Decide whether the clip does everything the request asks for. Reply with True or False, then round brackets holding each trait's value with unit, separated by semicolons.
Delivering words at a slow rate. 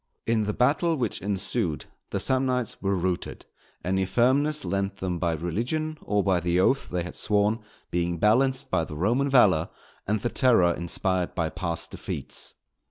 False (165 wpm)